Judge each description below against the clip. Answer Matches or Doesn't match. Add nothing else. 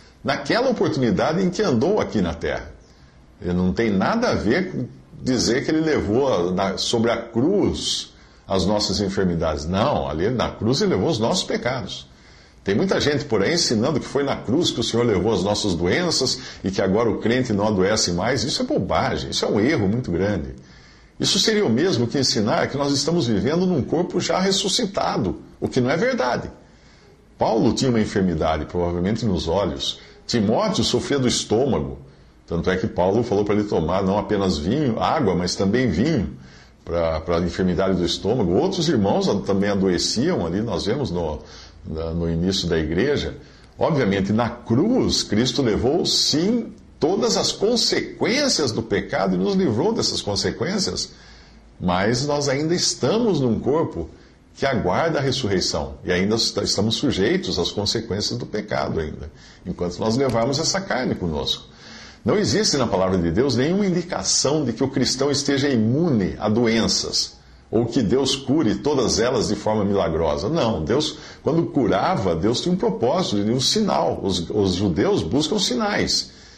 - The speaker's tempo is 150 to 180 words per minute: Matches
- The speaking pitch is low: Matches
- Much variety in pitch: Matches